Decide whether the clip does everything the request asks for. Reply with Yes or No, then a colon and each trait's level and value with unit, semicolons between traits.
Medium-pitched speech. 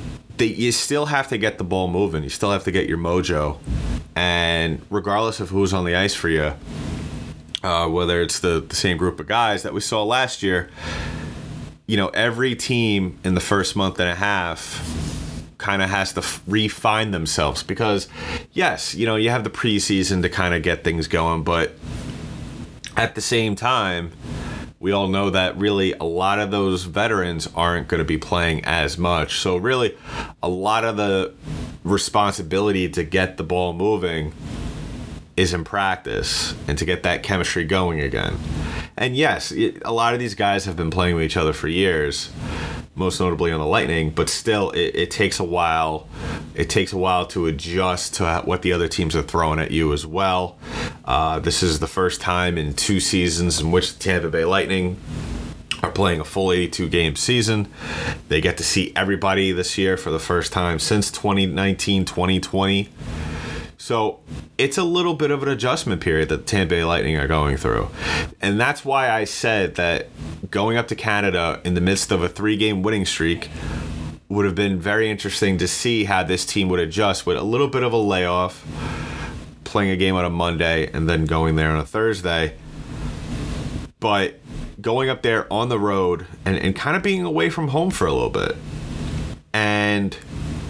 No: very low, 90 Hz